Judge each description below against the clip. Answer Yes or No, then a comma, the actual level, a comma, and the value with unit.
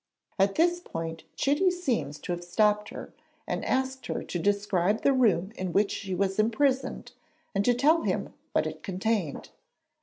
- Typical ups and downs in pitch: No, wide, 6.0 semitones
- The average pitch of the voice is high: Yes, high, 210 Hz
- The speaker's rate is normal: Yes, average, 170 wpm